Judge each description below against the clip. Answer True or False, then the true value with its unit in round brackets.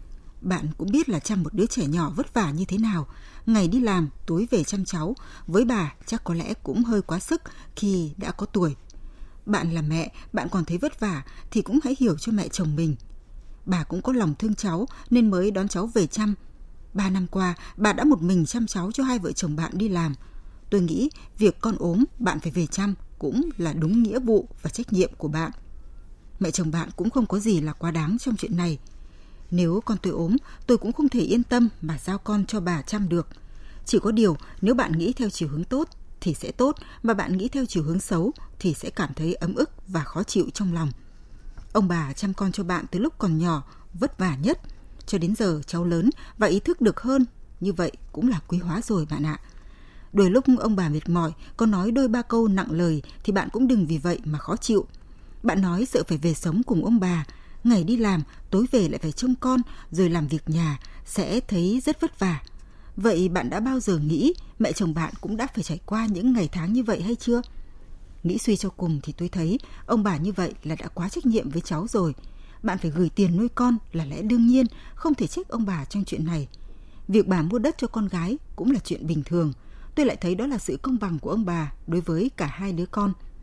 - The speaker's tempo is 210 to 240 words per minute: True (235 wpm)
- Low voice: False (190 Hz)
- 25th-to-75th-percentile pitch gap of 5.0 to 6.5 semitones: True (5.4 semitones)